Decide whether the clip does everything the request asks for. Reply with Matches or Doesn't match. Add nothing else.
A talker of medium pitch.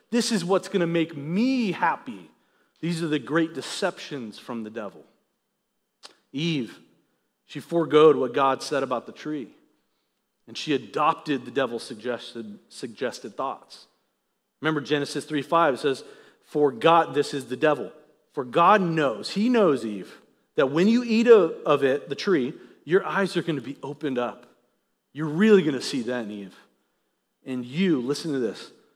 Matches